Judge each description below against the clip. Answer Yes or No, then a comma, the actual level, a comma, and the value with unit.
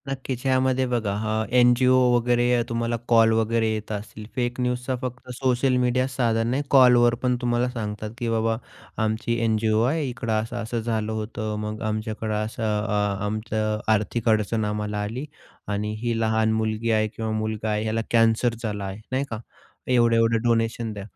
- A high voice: No, low, 115 Hz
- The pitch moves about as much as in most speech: No, narrow, 2.0 semitones